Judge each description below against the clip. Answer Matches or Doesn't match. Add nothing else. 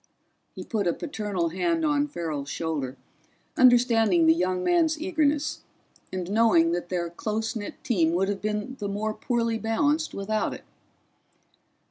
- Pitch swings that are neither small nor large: Doesn't match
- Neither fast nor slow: Matches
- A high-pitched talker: Matches